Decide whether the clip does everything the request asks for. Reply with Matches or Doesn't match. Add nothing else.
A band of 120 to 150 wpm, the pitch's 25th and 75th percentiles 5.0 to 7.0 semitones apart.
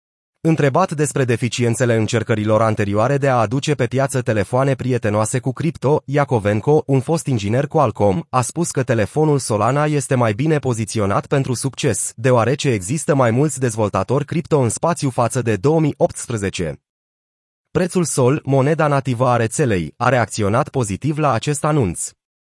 Doesn't match